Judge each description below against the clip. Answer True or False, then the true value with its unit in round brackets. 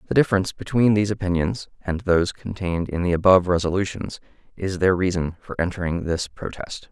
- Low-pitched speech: True (90 Hz)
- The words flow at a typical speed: True (165 wpm)